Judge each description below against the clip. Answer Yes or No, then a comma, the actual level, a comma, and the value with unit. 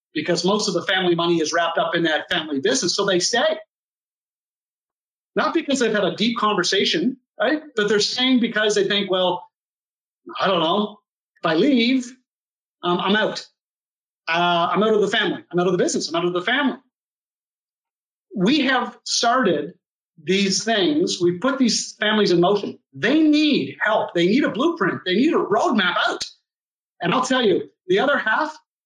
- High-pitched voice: Yes, high, 210 Hz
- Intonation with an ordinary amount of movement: No, wide, 6.5 semitones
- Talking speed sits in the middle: Yes, average, 180 wpm